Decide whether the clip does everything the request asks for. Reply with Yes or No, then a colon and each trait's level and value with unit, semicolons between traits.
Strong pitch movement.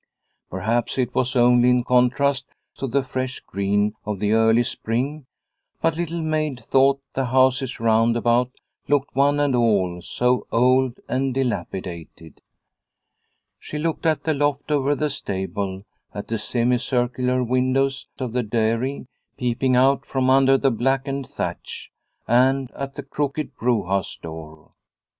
No: average, 3.1 semitones